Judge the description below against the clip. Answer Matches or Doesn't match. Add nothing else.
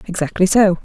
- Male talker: Doesn't match